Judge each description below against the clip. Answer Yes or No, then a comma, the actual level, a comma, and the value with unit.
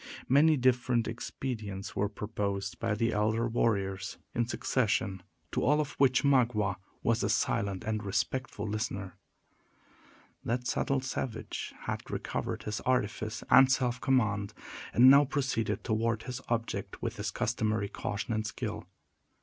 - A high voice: No, low, 115 Hz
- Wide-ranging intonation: No, average, 3.7 semitones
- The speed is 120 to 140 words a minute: Yes, slow, 135 wpm